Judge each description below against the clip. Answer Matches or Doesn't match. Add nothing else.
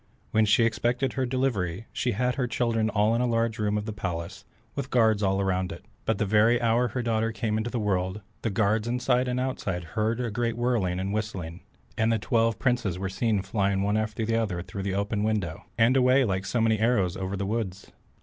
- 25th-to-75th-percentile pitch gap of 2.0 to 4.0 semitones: Matches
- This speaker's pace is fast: Matches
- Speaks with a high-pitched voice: Doesn't match